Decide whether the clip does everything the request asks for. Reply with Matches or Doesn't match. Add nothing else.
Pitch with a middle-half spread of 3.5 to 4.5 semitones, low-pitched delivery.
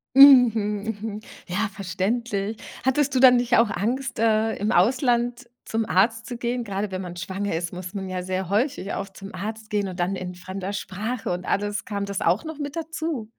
Doesn't match